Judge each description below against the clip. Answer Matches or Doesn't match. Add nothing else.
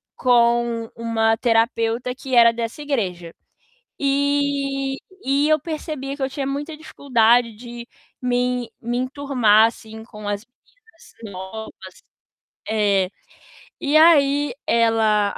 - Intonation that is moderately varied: Matches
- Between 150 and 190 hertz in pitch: Doesn't match